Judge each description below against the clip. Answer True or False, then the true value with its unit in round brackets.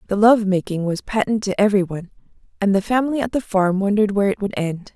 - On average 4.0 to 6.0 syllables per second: False (6.8 syllables/s)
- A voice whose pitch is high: True (200 Hz)